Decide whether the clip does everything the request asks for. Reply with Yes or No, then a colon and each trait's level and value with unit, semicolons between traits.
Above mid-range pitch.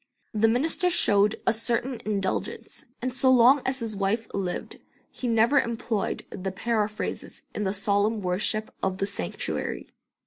Yes: high, 220 Hz